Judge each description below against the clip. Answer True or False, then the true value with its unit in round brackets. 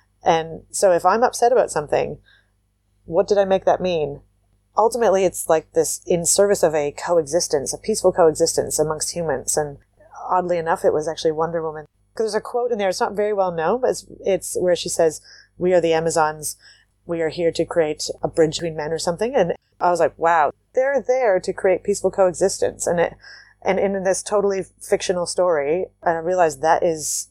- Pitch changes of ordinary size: True (3.3 semitones)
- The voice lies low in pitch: False (170 Hz)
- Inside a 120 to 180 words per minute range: False (200 wpm)